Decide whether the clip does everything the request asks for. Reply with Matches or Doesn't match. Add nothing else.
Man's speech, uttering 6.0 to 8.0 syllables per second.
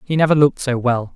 Matches